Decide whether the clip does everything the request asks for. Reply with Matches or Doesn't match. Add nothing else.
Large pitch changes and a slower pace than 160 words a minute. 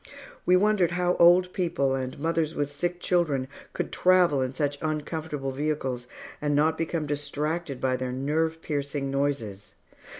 Doesn't match